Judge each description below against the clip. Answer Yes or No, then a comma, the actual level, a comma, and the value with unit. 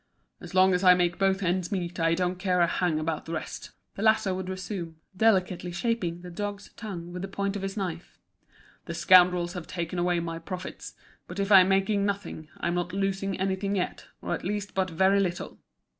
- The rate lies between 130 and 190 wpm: No, fast, 205 wpm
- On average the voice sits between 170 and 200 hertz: Yes, medium, 185 Hz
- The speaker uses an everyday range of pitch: No, narrow, 2.0 semitones